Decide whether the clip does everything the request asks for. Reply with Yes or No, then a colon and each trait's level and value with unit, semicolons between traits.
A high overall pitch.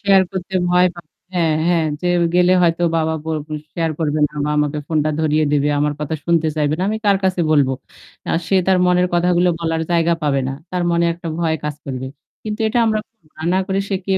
No: medium, 170 Hz